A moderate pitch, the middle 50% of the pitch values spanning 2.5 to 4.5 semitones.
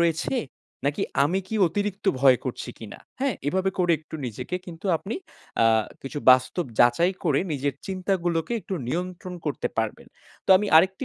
No: medium, 170 Hz; average, 5.1 semitones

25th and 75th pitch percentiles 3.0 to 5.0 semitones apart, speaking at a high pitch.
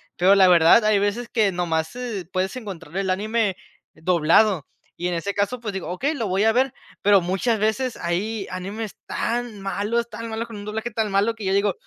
Yes: average, 3.3 semitones; high, 205 Hz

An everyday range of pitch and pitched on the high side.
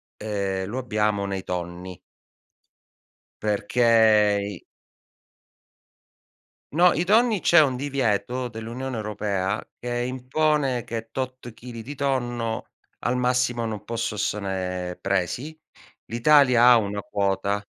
No: average, 3.9 semitones; low, 115 Hz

